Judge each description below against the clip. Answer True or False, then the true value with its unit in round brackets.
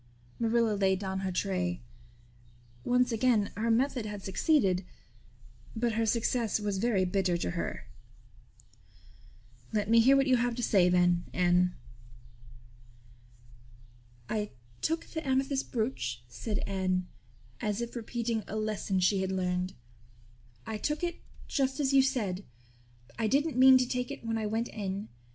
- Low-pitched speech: False (215 Hz)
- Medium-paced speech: True (145 wpm)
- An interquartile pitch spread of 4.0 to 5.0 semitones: True (4.5 semitones)